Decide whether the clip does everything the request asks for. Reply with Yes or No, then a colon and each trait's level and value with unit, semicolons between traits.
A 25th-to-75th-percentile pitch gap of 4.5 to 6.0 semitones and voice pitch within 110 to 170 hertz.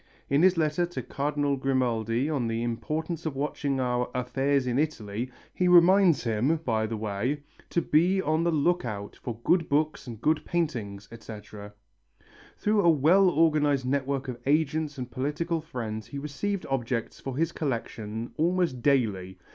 Yes: average, 5.1 semitones; medium, 140 Hz